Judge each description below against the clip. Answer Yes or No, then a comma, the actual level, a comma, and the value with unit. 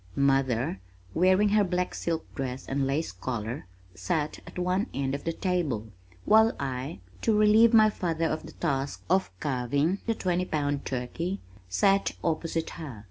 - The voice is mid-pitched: Yes, medium, 160 Hz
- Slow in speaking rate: No, average, 155 wpm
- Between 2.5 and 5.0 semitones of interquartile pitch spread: No, wide, 5.6 semitones